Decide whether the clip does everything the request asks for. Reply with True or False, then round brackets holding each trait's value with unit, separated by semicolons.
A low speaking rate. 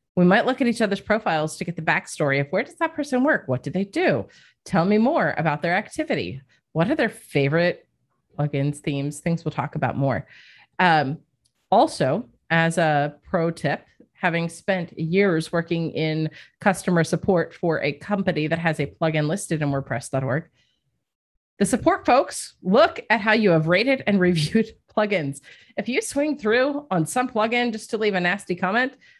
False (175 wpm)